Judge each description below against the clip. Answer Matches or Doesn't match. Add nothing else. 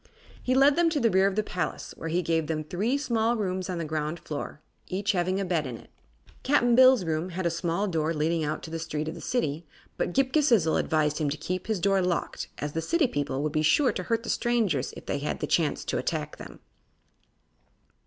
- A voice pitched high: Doesn't match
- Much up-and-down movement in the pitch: Matches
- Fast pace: Matches